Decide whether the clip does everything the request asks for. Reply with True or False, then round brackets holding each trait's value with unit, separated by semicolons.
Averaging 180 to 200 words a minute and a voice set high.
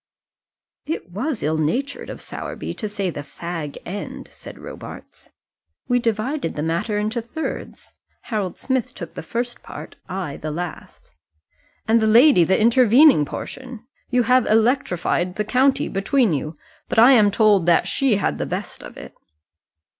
False (160 wpm; 215 Hz)